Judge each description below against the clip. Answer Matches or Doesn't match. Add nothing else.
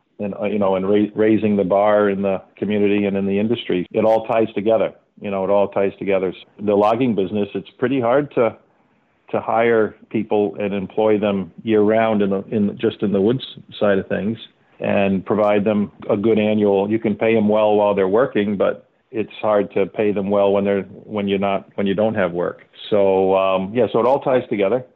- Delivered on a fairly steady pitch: Matches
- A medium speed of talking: Doesn't match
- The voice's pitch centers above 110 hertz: Doesn't match